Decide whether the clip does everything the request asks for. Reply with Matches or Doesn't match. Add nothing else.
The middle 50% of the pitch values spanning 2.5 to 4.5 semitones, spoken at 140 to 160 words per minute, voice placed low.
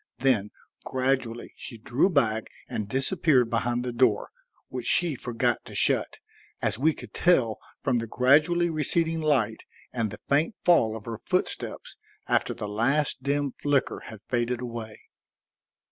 Matches